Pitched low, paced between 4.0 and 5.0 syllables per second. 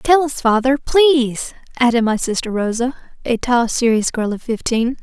No: high, 245 Hz; 4.8 syllables/s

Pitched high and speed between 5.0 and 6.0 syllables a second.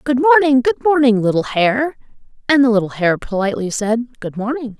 Yes: high, 240 Hz; 5.3 syllables/s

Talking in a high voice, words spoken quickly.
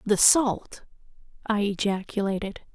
No: high, 205 Hz; slow, 85 wpm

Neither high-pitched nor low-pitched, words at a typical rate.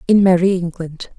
Yes: medium, 180 Hz; average, 150 wpm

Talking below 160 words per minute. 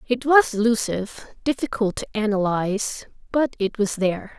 Yes: slow, 135 wpm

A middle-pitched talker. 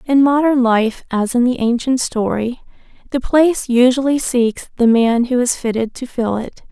No: high, 245 Hz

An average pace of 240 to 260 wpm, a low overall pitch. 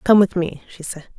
No: fast, 255 wpm; medium, 180 Hz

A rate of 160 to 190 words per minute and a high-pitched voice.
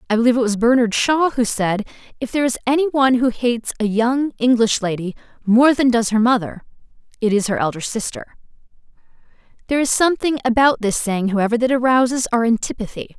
Yes: average, 180 wpm; high, 240 Hz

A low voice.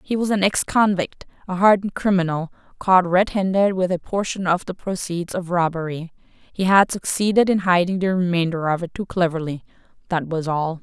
No: medium, 180 Hz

